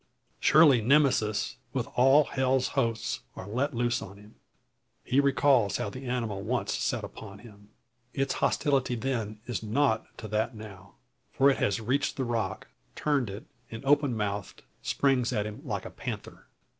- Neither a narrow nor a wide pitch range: Yes, average, 4.1 semitones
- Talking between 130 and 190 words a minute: Yes, average, 160 wpm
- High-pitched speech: No, low, 120 Hz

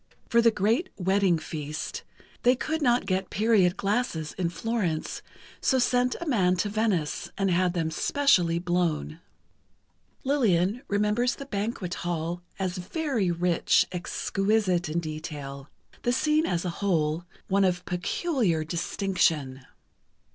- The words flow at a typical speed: No, slow, 125 wpm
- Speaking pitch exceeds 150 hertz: Yes, medium, 185 Hz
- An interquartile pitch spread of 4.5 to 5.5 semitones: Yes, average, 5.1 semitones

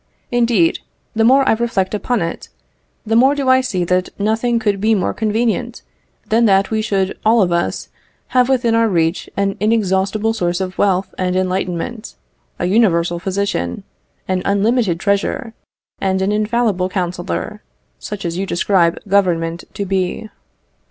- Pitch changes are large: No, average, 3.6 semitones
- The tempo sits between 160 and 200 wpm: No, average, 150 wpm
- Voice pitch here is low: No, high, 200 Hz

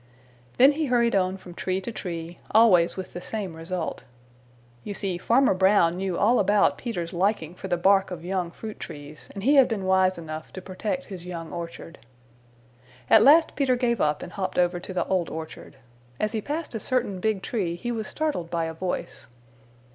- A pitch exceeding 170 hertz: Yes, high, 190 Hz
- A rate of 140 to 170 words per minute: No, average, 195 wpm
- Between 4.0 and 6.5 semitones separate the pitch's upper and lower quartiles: Yes, average, 4.3 semitones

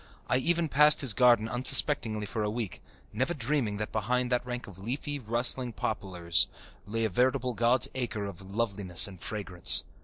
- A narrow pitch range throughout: No, average, 3.7 semitones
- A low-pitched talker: Yes, low, 115 Hz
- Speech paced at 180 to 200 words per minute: No, average, 165 wpm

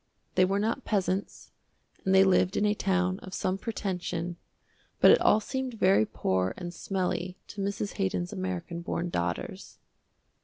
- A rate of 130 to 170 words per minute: Yes, average, 155 wpm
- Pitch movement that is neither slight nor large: No, narrow, 2.2 semitones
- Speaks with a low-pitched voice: No, medium, 185 Hz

